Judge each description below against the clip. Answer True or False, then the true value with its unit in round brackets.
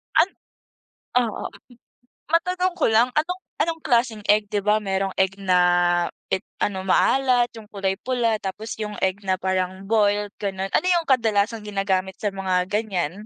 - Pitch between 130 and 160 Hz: False (210 Hz)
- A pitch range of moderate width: True (3.6 semitones)